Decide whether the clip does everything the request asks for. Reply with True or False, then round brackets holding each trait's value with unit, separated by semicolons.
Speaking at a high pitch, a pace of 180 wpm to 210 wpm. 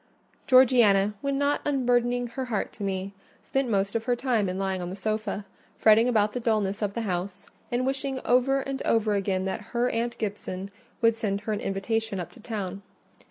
True (220 Hz; 195 wpm)